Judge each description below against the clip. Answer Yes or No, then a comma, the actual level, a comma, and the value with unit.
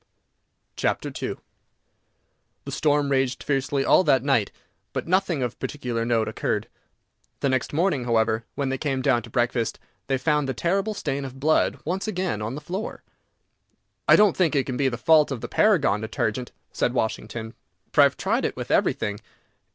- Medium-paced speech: Yes, average, 175 wpm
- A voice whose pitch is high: No, low, 135 Hz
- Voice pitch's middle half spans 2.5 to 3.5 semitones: No, average, 4.6 semitones